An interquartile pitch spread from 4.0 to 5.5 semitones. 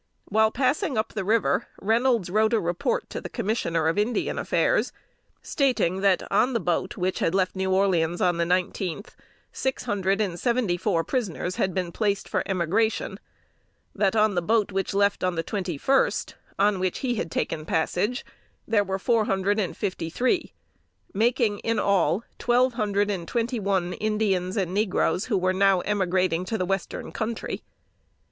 No: average, 3.3 semitones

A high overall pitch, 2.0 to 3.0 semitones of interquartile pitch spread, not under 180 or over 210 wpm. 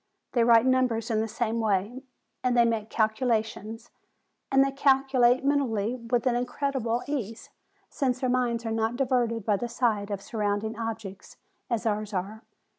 No: high, 230 Hz; narrow, 2.6 semitones; average, 165 wpm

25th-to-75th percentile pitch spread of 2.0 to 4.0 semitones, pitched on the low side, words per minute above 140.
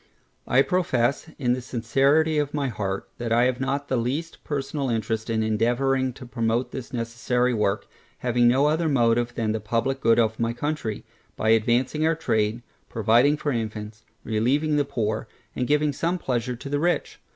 Yes: average, 3.6 semitones; low, 125 Hz; average, 175 wpm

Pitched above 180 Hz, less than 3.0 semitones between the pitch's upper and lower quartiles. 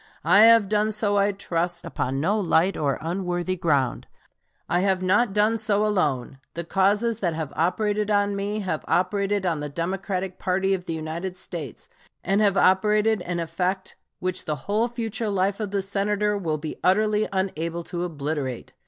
No: high, 190 Hz; average, 3.4 semitones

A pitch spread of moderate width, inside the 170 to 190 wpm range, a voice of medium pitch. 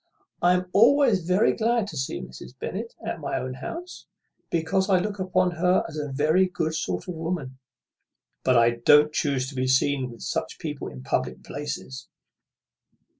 No: wide, 6.1 semitones; average, 175 wpm; medium, 160 Hz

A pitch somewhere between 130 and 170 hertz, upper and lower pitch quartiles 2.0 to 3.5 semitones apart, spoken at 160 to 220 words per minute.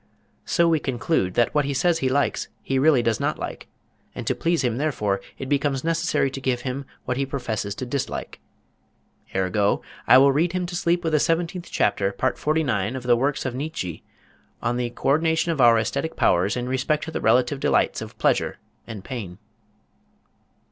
No: low, 135 Hz; average, 4.7 semitones; average, 195 wpm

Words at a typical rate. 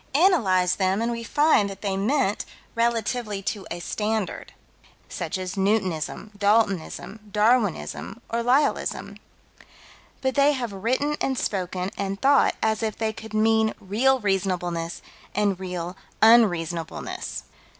No: slow, 125 wpm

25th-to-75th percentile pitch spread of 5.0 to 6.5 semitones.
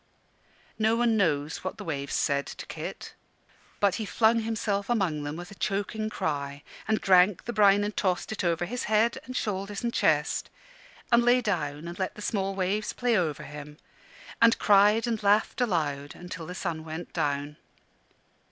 Yes: wide, 5.5 semitones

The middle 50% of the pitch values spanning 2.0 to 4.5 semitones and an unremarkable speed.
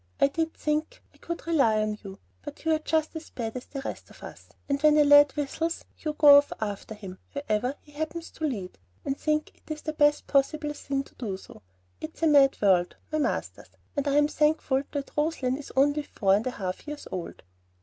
No: average, 3.7 semitones; fast, 210 wpm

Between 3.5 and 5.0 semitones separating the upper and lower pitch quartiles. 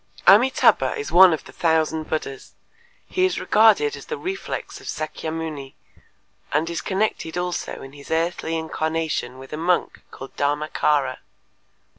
Yes: average, 3.9 semitones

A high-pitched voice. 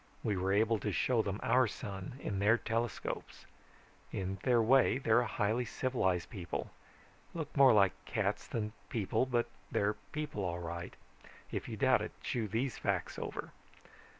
No: low, 110 Hz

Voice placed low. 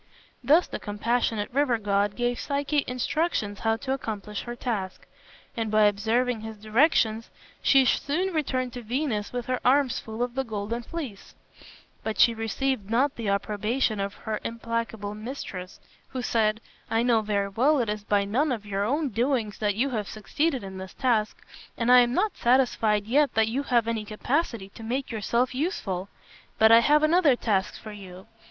No: high, 230 Hz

